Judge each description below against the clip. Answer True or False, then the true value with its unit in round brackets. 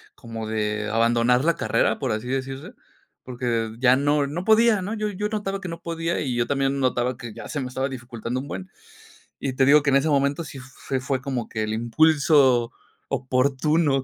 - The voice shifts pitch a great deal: False (4.0 semitones)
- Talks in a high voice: False (135 Hz)